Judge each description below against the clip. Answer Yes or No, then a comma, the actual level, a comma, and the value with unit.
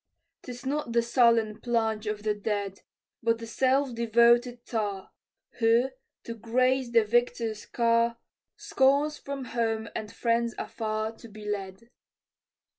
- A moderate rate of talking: No, slow, 130 wpm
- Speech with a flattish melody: Yes, narrow, 1.9 semitones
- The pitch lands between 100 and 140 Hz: No, high, 230 Hz